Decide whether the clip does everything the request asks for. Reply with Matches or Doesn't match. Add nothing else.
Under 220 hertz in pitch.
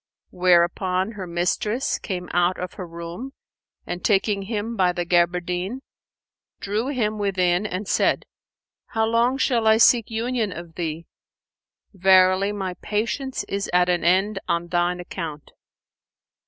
Matches